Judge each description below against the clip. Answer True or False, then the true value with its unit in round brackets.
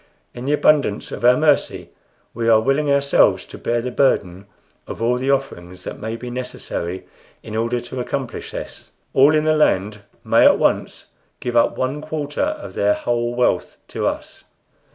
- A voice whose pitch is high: False (125 Hz)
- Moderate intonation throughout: True (3.7 semitones)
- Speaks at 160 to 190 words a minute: True (175 wpm)